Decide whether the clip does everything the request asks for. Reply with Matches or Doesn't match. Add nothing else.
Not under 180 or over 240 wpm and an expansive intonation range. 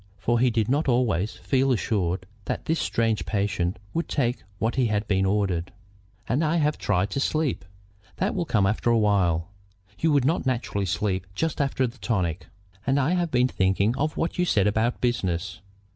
Matches